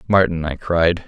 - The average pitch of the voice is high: No, very low, 85 Hz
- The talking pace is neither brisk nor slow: Yes, average, 170 wpm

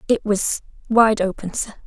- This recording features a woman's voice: Yes, female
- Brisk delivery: No, average, 160 wpm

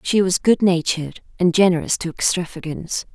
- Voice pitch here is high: No, medium, 175 Hz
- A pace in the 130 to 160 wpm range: Yes, slow, 135 wpm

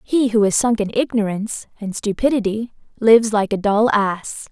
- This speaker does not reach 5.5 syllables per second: Yes, 5.0 syllables/s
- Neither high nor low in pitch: No, high, 215 Hz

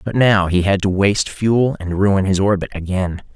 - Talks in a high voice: No, low, 100 Hz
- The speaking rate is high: Yes, fast, 215 wpm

